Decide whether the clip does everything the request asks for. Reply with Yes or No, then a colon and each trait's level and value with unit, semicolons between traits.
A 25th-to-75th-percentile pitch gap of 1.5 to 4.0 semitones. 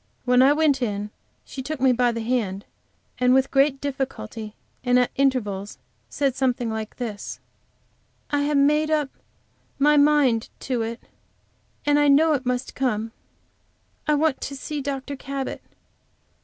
Yes: average, 3.2 semitones